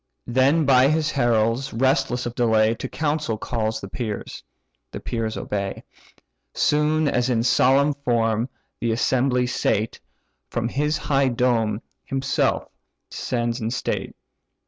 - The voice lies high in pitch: No, low, 125 Hz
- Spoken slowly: Yes, slow, 125 wpm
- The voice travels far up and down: No, average, 3.2 semitones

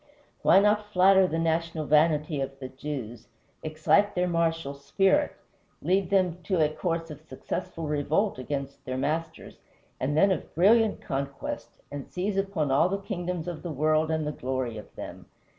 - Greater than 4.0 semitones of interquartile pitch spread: Yes, average, 4.4 semitones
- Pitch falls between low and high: Yes, medium, 160 Hz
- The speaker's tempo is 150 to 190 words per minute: Yes, average, 165 wpm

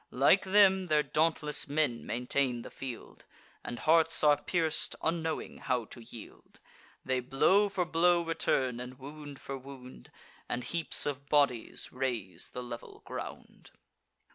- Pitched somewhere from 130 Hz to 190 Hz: Yes, medium, 140 Hz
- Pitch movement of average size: Yes, average, 4.5 semitones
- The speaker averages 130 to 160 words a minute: Yes, average, 140 wpm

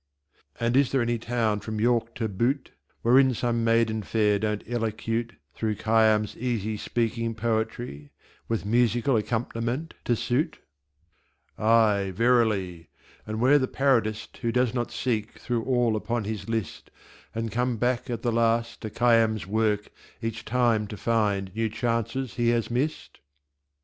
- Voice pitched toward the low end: Yes, low, 115 Hz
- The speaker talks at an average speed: Yes, average, 145 wpm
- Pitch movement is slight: Yes, narrow, 1.8 semitones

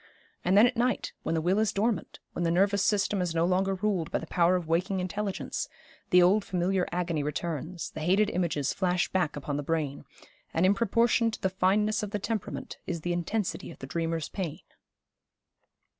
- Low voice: No, medium, 185 Hz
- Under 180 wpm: No, average, 195 wpm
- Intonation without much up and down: No, average, 3.2 semitones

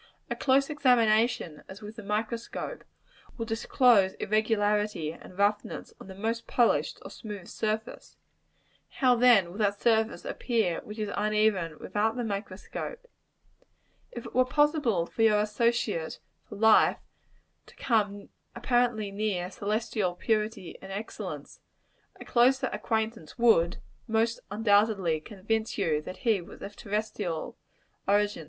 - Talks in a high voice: Yes, high, 215 Hz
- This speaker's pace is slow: Yes, slow, 130 wpm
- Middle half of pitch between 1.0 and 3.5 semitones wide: Yes, narrow, 2.6 semitones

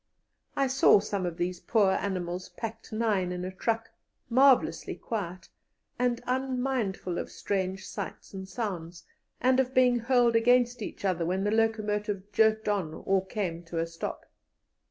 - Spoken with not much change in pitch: No, average, 4.3 semitones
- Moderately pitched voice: No, high, 205 Hz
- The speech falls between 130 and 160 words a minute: Yes, average, 155 wpm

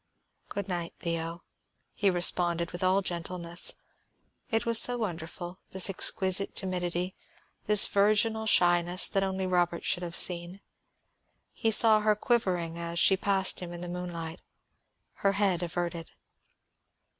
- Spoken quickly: No, slow, 135 wpm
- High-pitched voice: No, medium, 180 Hz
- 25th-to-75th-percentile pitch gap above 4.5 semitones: No, narrow, 2.4 semitones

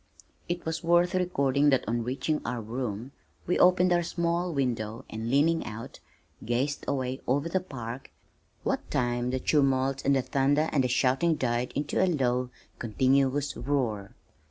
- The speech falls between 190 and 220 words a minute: No, average, 155 wpm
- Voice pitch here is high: No, low, 135 Hz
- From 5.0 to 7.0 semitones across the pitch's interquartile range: No, average, 4.3 semitones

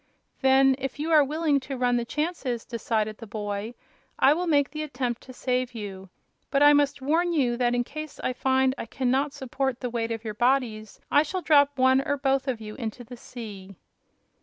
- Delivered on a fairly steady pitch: No, average, 3.4 semitones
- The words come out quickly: Yes, fast, 210 wpm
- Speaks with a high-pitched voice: Yes, very high, 260 Hz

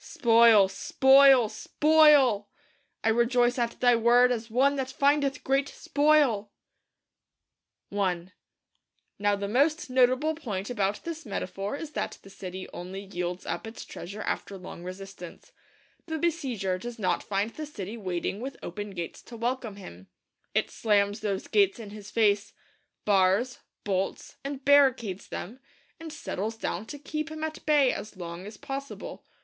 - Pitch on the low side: No, high, 225 Hz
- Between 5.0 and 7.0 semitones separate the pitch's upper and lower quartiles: Yes, wide, 5.5 semitones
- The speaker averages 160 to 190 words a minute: No, average, 150 wpm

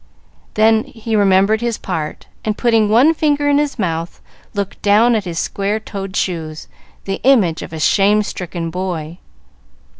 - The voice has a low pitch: No, high, 200 Hz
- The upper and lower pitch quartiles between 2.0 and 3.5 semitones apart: No, average, 3.9 semitones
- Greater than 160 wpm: No, average, 155 wpm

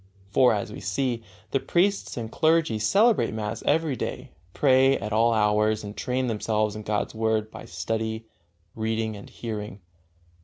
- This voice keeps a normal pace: Yes, average, 155 wpm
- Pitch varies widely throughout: No, average, 3.4 semitones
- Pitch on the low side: Yes, low, 110 Hz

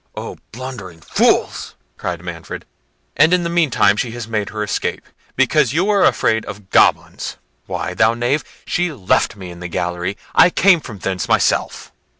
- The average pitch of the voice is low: Yes, low, 110 Hz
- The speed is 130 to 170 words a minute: Yes, average, 160 wpm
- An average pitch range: No, wide, 8.3 semitones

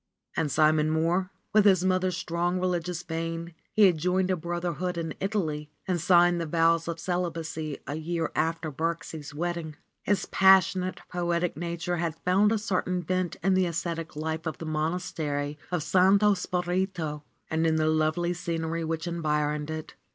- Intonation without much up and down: Yes, narrow, 2.3 semitones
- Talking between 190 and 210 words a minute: No, average, 160 wpm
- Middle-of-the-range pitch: Yes, medium, 170 Hz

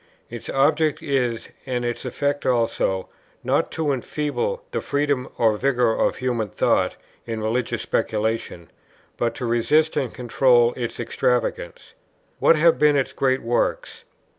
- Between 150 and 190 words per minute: No, average, 140 wpm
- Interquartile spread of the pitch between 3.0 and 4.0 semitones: Yes, average, 3.5 semitones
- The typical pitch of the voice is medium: No, low, 125 Hz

